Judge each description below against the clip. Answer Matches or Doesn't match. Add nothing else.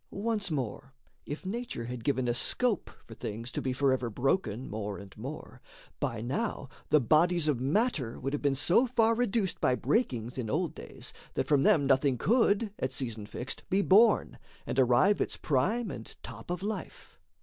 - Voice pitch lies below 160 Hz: Matches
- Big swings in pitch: Matches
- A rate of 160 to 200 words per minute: Matches